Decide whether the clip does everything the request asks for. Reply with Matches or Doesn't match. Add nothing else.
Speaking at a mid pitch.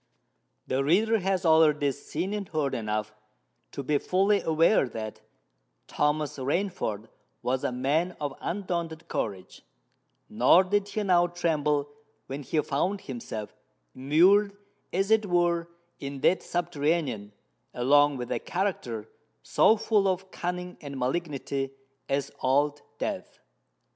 Matches